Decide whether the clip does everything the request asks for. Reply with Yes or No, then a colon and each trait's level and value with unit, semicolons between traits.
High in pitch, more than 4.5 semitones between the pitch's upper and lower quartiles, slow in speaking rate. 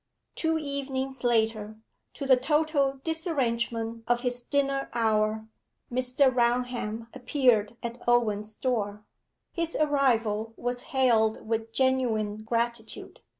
No: high, 240 Hz; average, 3.2 semitones; slow, 105 wpm